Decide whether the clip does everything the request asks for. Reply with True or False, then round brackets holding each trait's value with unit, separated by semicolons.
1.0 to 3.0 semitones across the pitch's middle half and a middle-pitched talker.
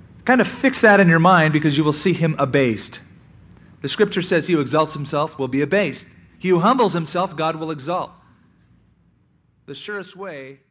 False (4.6 semitones; 160 Hz)